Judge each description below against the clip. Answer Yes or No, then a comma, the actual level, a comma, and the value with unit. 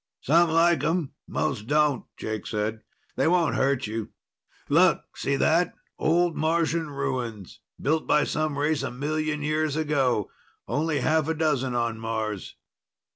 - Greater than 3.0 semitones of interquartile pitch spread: Yes, average, 4.4 semitones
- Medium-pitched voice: Yes, medium, 150 Hz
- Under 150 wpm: Yes, average, 140 wpm